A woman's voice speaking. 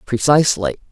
Yes: female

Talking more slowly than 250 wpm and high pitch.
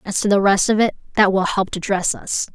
No: fast, 285 wpm; high, 200 Hz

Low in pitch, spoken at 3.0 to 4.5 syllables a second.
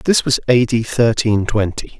Yes: low, 115 Hz; 4.3 syllables/s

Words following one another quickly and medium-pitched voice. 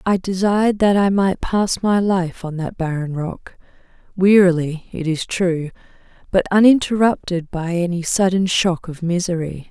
No: average, 150 wpm; medium, 180 Hz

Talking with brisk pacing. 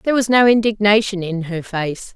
No: average, 195 wpm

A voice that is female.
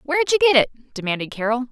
Yes: female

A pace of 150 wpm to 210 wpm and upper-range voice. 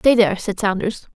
Yes: fast, 205 wpm; high, 205 Hz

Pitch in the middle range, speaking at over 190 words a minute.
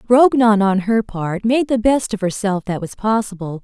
No: high, 210 Hz; average, 200 wpm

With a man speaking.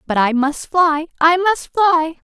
No: female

